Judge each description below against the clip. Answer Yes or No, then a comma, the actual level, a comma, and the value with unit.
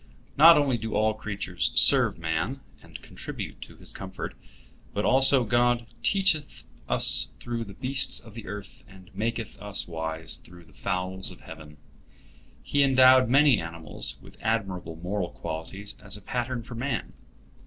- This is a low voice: Yes, low, 105 Hz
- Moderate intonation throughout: No, wide, 6.1 semitones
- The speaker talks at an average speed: Yes, average, 155 wpm